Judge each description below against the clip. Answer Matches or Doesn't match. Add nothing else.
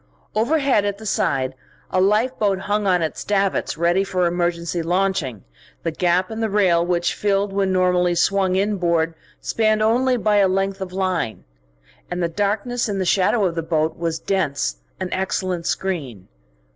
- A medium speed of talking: Matches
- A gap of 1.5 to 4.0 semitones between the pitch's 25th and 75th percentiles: Matches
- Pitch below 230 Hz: Matches